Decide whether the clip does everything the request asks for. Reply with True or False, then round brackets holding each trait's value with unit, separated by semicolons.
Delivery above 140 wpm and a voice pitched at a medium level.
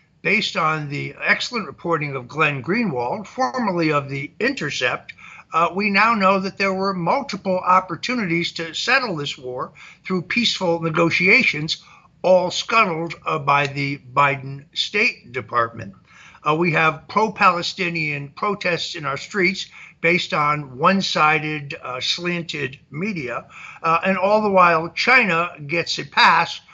False (135 wpm; 170 Hz)